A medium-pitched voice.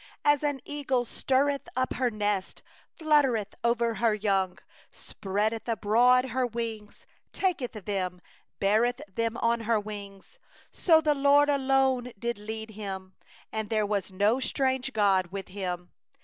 No: high, 230 Hz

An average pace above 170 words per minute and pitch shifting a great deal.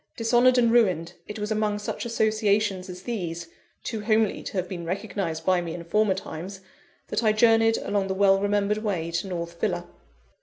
No: average, 185 wpm; average, 3.2 semitones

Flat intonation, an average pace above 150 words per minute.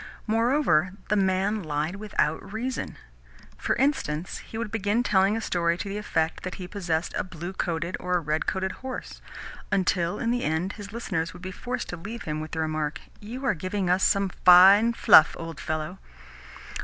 No: average, 4.2 semitones; average, 185 wpm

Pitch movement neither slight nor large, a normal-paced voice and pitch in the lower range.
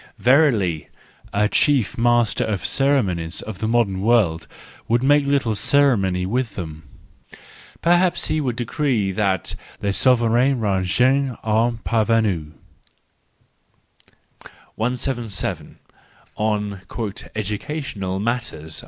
No: average, 4.6 semitones; slow, 100 wpm; low, 110 Hz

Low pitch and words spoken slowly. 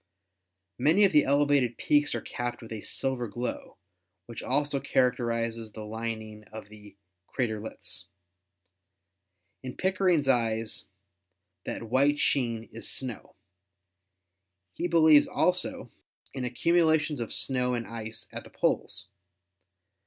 Yes: low, 125 Hz; slow, 120 wpm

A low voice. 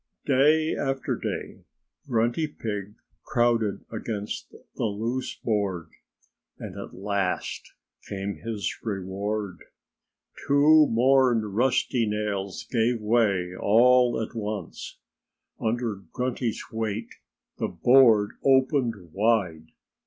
Yes: low, 110 Hz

